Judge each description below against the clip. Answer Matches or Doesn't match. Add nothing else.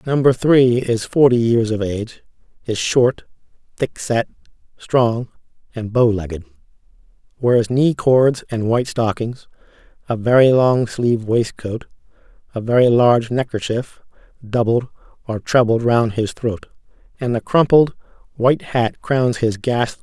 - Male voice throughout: Matches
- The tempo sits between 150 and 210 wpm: Doesn't match